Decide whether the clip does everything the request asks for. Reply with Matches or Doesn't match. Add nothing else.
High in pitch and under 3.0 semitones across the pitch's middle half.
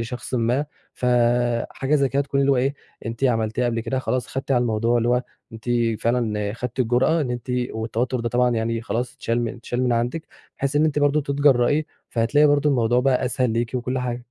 Doesn't match